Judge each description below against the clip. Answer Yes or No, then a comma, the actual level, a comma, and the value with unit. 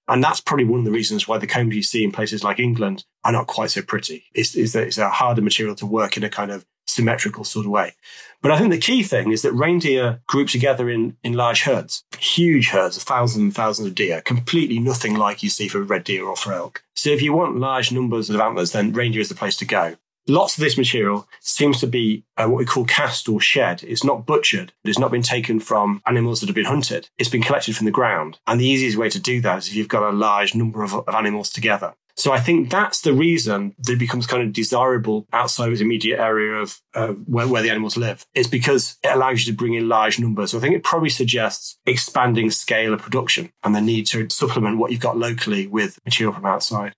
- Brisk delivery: Yes, fast, 250 wpm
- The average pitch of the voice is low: Yes, low, 115 Hz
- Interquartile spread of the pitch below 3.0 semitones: Yes, narrow, 2.6 semitones